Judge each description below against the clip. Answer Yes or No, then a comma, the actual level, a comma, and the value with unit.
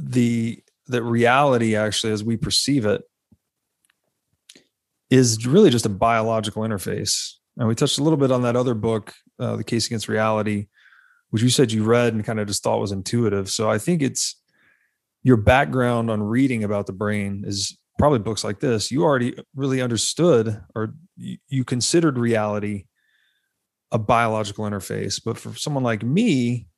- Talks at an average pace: Yes, average, 165 wpm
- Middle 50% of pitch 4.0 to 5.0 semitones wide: No, average, 2.8 semitones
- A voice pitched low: Yes, low, 115 Hz